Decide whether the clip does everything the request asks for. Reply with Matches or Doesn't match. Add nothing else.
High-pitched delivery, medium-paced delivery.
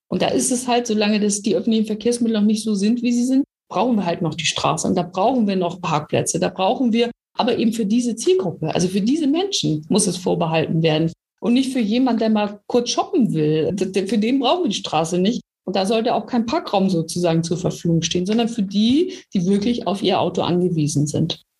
Doesn't match